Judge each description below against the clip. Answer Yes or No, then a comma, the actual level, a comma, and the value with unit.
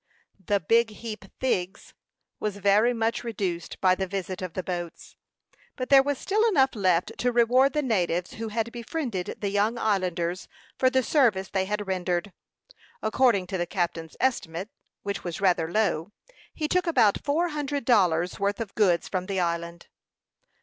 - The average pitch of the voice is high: Yes, high, 205 Hz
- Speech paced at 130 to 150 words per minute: No, average, 165 wpm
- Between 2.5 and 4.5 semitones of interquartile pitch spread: No, average, 4.9 semitones